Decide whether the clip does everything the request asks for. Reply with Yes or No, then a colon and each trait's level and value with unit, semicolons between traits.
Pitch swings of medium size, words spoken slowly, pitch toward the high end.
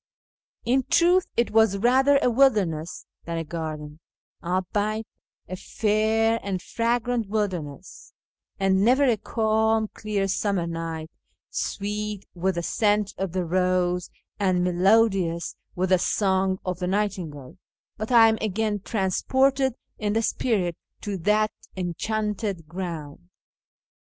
Yes: average, 3.6 semitones; slow, 130 wpm; high, 200 Hz